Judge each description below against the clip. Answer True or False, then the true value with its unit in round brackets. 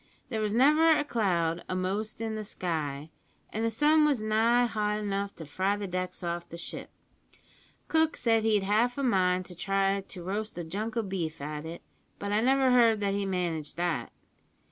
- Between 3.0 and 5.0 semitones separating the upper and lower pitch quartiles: True (4.0 semitones)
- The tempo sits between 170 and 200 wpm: True (190 wpm)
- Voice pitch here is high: True (200 Hz)